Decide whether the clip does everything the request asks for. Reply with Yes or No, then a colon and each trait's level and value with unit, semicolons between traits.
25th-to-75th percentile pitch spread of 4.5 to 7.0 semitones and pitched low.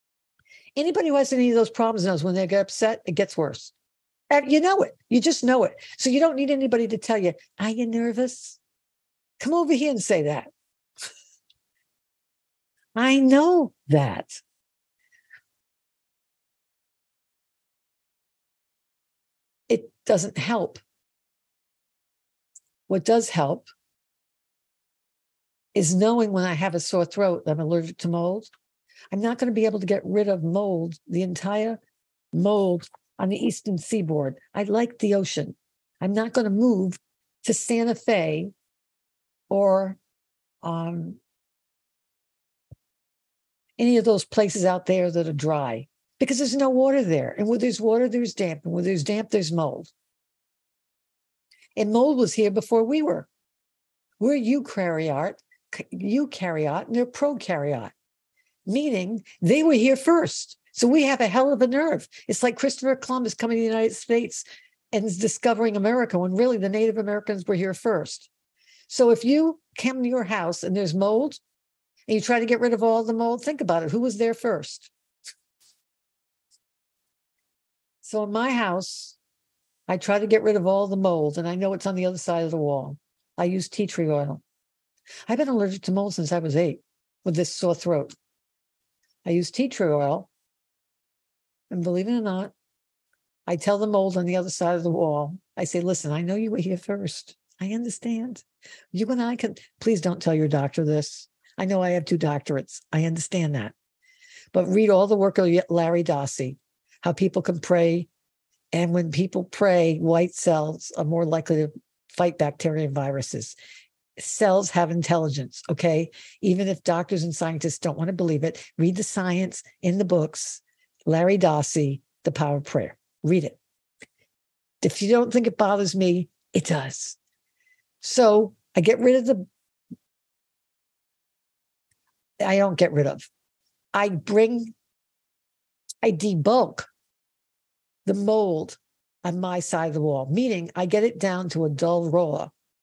No: average, 5.3 semitones; high, 195 Hz